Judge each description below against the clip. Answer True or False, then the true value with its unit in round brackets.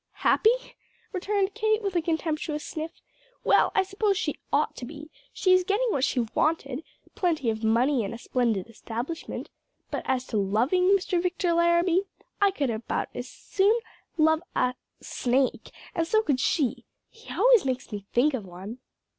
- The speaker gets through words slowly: False (165 wpm)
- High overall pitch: True (310 Hz)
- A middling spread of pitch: False (6.9 semitones)